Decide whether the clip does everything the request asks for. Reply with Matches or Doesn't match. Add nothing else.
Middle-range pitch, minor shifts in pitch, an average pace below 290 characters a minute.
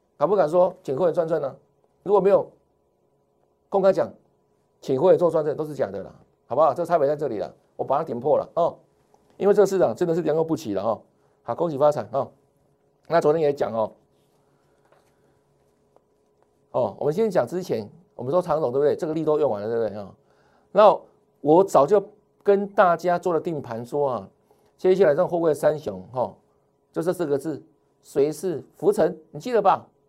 Doesn't match